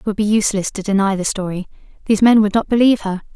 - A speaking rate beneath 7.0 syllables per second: No, 7.4 syllables/s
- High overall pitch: Yes, high, 205 Hz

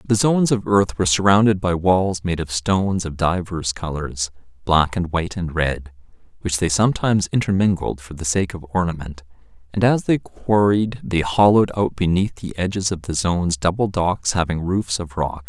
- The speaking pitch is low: Yes, very low, 90 Hz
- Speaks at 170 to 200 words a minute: Yes, average, 180 wpm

